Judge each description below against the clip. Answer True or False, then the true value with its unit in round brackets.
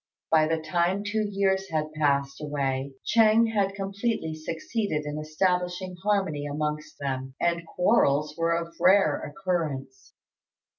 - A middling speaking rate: False (130 wpm)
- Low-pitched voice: False (165 Hz)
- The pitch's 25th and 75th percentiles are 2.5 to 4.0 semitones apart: False (4.5 semitones)